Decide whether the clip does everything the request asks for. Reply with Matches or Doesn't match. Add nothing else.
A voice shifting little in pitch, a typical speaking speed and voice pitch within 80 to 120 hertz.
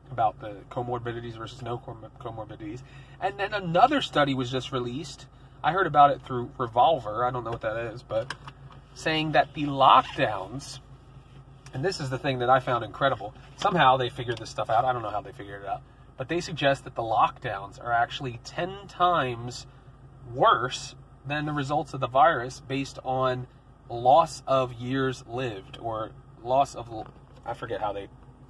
Doesn't match